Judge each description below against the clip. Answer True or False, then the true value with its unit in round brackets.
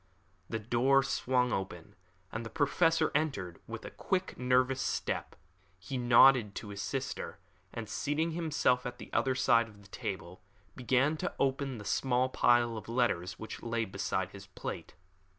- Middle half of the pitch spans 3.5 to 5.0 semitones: True (4.3 semitones)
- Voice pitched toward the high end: False (120 Hz)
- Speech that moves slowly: False (160 wpm)